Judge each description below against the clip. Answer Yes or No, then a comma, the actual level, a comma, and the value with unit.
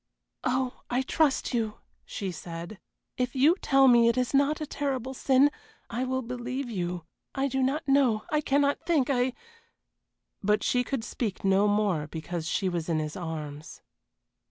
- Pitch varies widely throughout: Yes, wide, 6.0 semitones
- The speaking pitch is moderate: No, high, 245 Hz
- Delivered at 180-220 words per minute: No, average, 170 wpm